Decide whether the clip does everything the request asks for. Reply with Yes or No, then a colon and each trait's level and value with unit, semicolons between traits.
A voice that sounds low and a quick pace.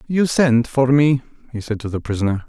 Yes: low, 125 Hz; fast, 220 wpm